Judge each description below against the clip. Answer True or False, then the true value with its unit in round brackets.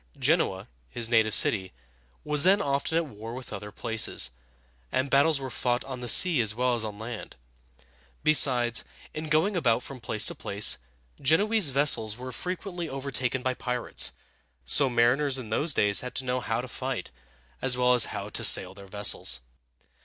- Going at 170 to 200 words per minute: True (175 wpm)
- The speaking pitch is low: True (125 Hz)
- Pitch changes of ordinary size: True (4.0 semitones)